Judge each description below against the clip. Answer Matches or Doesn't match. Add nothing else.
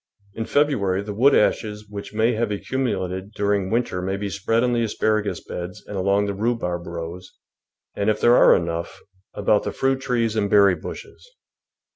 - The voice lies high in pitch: Doesn't match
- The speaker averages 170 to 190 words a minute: Matches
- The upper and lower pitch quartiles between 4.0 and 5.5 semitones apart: Doesn't match